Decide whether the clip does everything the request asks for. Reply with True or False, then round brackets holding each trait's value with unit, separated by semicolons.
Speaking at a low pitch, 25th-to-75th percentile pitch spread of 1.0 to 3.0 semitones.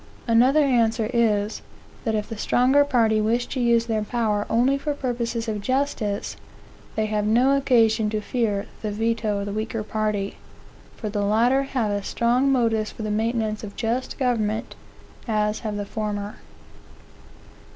False (225 Hz; 2.4 semitones)